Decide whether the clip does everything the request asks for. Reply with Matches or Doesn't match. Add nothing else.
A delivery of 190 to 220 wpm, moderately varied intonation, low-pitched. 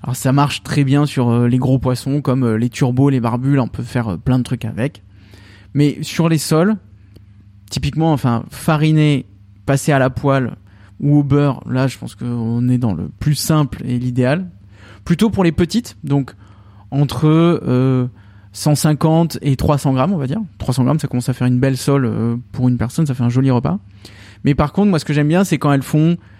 Matches